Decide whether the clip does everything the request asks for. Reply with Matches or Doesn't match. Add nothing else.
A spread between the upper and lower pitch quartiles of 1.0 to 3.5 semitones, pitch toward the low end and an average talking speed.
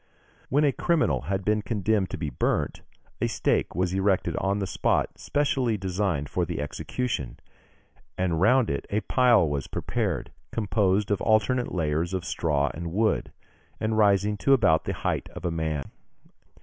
Doesn't match